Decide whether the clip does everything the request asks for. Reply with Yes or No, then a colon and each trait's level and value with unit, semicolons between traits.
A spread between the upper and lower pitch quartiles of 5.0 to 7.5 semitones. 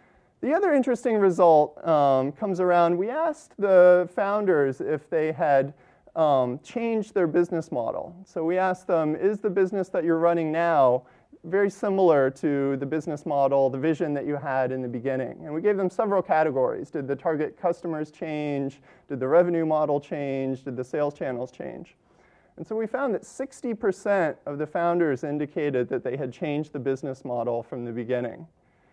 Yes: average, 5.3 semitones